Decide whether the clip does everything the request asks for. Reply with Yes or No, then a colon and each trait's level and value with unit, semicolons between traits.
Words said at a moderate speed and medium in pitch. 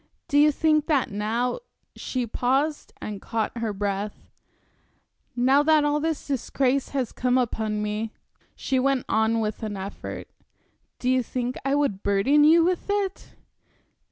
No: average, 150 wpm; very high, 255 Hz